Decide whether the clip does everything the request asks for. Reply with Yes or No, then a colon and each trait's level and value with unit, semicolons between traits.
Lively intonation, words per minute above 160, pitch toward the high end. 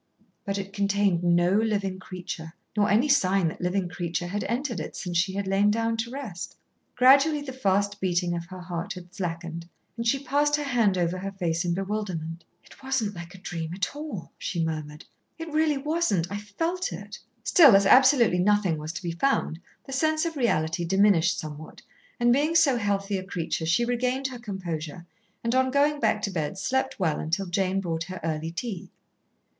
Yes: wide, 6.0 semitones; average, 190 wpm; high, 195 Hz